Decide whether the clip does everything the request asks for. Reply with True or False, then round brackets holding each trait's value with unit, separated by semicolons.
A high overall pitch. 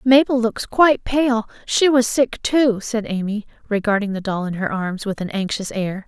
True (220 Hz)